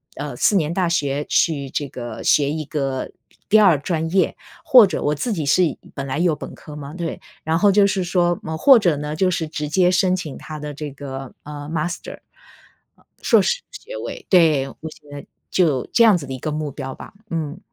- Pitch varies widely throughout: No, average, 4.0 semitones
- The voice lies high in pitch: No, medium, 155 Hz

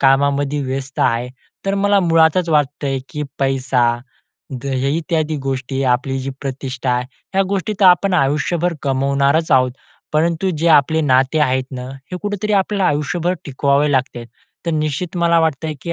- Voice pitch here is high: No, medium, 145 Hz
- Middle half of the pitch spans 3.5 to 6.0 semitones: Yes, average, 3.9 semitones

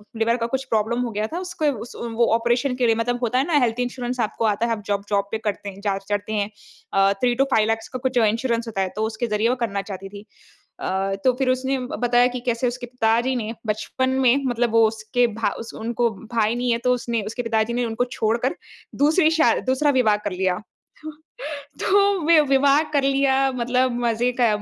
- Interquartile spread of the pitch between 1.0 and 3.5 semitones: Yes, average, 2.7 semitones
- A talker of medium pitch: No, high, 235 Hz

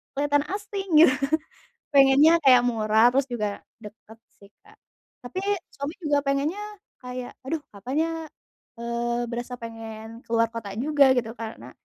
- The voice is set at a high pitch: Yes, high, 245 Hz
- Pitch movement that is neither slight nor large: Yes, average, 3.7 semitones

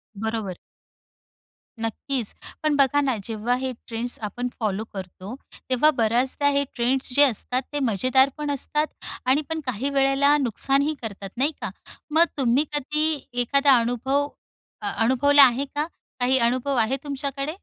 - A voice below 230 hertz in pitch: No, very high, 260 Hz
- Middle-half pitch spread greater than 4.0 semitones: No, average, 3.4 semitones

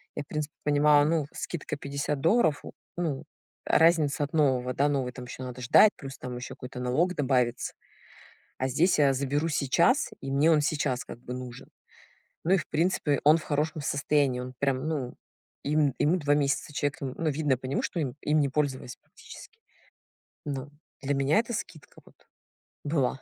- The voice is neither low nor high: Yes, medium, 145 Hz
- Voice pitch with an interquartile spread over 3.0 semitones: No, average, 2.7 semitones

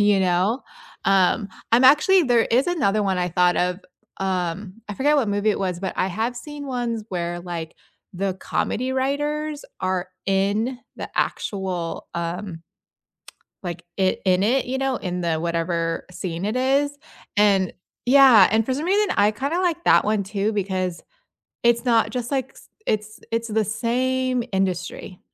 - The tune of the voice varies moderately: No, wide, 5.7 semitones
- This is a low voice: No, high, 210 Hz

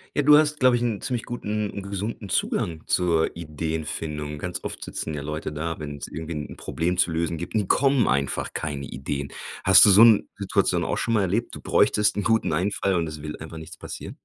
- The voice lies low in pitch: Yes, very low, 85 Hz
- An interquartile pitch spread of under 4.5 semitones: No, wide, 5.4 semitones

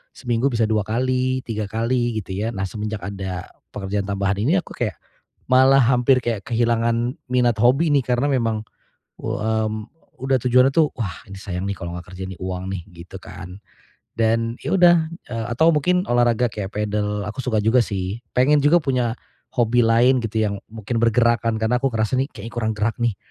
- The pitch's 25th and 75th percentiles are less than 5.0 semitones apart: Yes, average, 3.5 semitones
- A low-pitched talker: Yes, low, 115 Hz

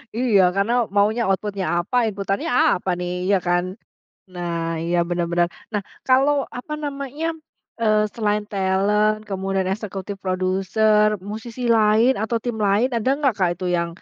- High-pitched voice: Yes, high, 205 Hz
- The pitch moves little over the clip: No, average, 3.1 semitones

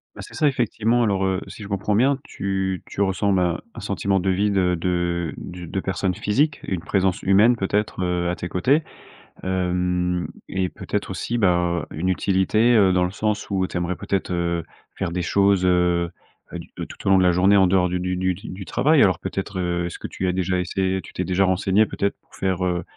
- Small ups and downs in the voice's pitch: Yes, narrow, 1.9 semitones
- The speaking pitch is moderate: No, very low, 95 Hz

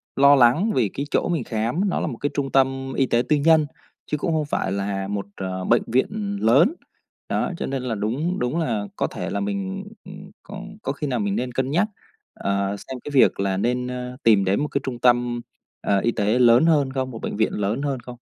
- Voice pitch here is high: No, low, 130 Hz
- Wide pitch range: No, average, 4.7 semitones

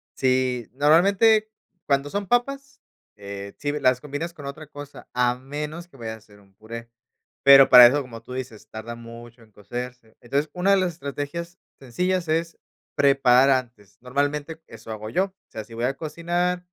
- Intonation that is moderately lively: No, wide, 5.9 semitones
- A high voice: No, low, 135 Hz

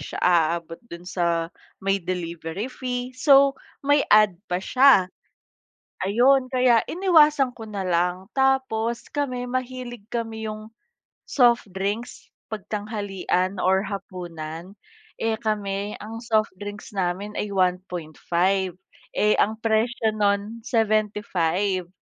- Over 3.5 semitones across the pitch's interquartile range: Yes, average, 4.4 semitones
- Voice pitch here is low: No, high, 210 Hz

